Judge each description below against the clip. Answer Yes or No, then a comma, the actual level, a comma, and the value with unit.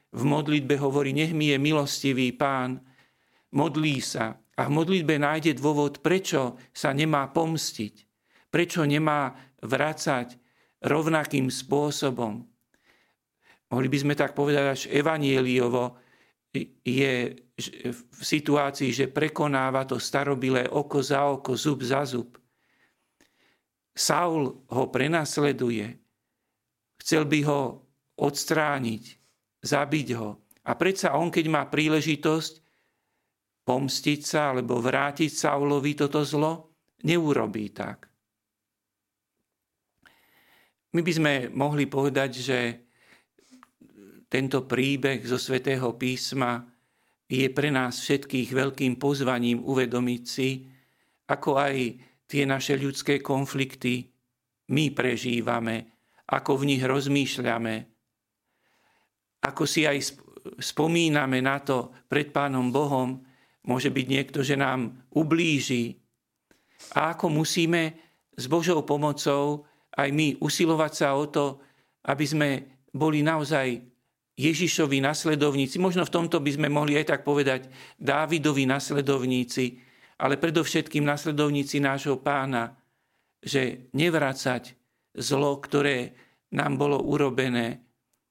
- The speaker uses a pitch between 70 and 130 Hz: No, medium, 140 Hz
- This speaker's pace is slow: Yes, slow, 105 wpm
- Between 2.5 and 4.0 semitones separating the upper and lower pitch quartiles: Yes, average, 2.8 semitones